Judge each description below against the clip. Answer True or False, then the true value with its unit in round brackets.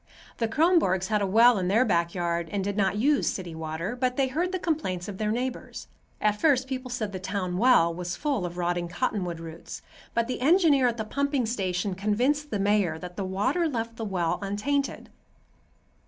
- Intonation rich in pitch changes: True (5.9 semitones)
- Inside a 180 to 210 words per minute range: True (200 wpm)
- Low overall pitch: False (210 Hz)